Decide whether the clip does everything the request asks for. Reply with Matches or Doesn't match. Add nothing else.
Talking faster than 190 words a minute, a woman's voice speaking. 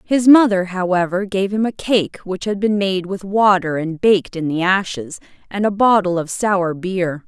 Matches